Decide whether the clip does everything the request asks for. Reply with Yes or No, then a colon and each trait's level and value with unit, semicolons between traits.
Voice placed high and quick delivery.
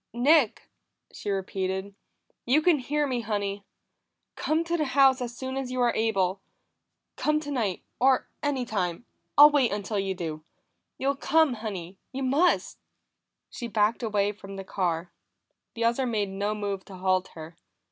No: high, 220 Hz; average, 155 wpm